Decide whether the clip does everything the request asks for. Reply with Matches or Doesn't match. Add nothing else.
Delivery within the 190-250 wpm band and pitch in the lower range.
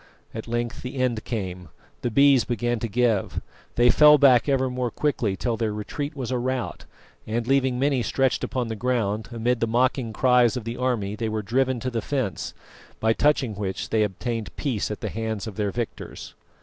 Matches